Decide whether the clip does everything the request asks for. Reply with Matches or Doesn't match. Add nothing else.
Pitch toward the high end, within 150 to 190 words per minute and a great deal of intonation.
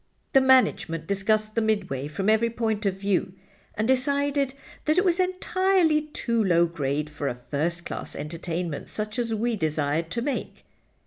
Matches